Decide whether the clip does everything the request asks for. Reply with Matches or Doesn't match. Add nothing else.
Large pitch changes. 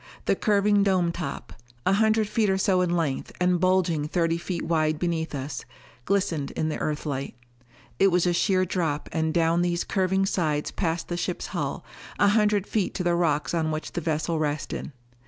Doesn't match